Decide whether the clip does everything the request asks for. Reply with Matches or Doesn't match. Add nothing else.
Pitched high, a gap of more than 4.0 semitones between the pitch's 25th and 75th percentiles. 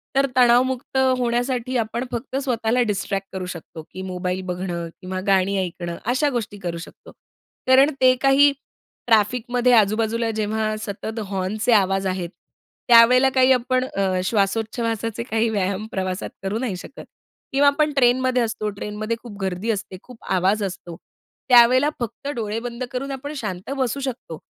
Matches